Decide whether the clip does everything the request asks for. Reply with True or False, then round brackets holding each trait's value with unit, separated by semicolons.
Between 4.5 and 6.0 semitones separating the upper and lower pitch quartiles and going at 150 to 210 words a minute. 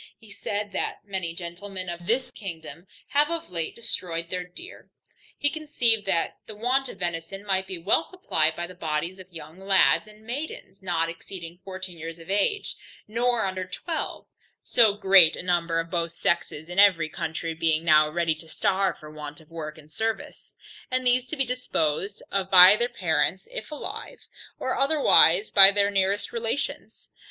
True (4.9 semitones; 175 wpm)